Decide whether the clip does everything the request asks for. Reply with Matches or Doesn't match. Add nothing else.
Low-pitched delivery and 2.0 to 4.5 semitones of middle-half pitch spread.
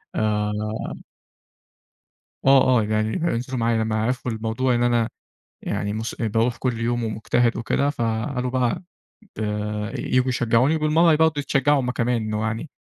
Matches